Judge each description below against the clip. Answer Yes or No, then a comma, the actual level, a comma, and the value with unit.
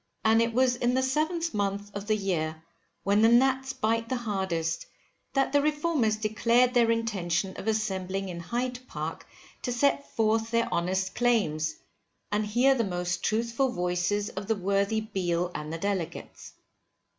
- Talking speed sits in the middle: Yes, average, 160 wpm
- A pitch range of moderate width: Yes, average, 4.3 semitones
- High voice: Yes, high, 215 Hz